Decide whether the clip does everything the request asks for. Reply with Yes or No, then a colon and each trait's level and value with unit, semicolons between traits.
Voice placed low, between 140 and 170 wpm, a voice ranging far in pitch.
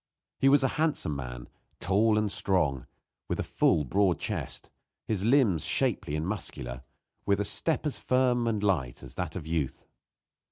Yes: low, 100 Hz; average, 165 wpm; wide, 7.3 semitones